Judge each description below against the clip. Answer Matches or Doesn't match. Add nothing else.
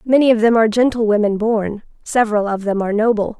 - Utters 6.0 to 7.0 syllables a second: Matches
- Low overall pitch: Doesn't match